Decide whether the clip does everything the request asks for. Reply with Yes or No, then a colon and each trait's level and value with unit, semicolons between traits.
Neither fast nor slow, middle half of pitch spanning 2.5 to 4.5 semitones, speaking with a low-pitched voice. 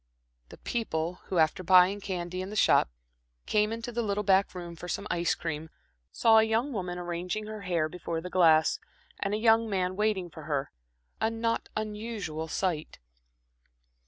No: average, 170 wpm; average, 4.0 semitones; medium, 185 Hz